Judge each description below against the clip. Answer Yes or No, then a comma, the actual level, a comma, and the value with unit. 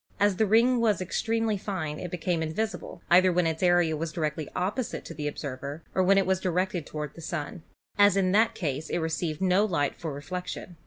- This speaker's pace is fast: Yes, fast, 210 wpm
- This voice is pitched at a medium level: Yes, medium, 180 Hz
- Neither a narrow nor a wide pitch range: Yes, average, 3.7 semitones